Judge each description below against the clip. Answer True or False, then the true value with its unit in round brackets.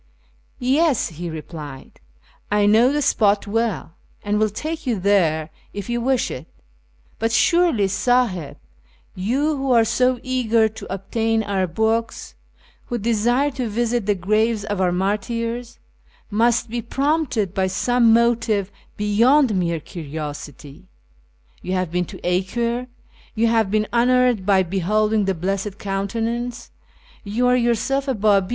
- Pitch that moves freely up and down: False (3.8 semitones)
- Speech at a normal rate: True (145 wpm)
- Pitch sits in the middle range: False (220 Hz)